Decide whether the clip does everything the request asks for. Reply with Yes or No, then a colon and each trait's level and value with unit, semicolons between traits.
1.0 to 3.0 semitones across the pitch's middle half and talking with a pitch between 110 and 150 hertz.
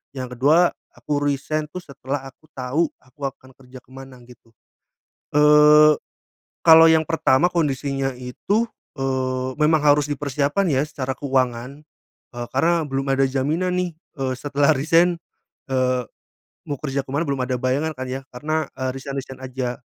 Yes: average, 2.7 semitones; medium, 140 Hz